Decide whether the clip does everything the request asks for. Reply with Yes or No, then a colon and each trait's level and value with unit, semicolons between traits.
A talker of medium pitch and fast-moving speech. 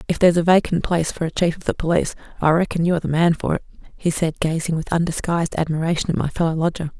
Yes: medium, 165 Hz; fast, 250 wpm